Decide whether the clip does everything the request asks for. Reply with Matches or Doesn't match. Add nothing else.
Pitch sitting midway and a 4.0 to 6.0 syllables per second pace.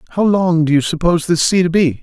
Doesn't match